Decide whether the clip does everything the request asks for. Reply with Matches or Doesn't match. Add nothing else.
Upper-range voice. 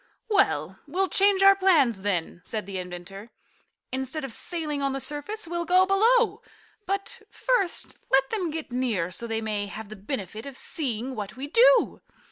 Matches